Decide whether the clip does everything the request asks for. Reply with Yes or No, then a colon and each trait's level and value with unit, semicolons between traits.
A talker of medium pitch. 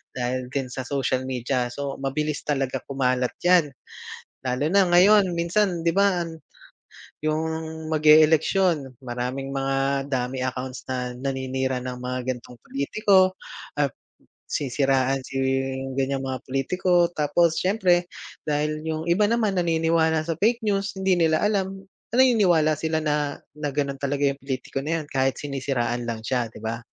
Yes: medium, 145 Hz